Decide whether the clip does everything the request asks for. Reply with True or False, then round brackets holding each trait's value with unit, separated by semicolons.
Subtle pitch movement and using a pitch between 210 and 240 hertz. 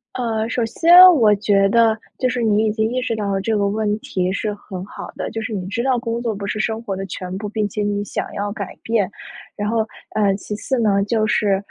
True (2.2 semitones; 215 Hz)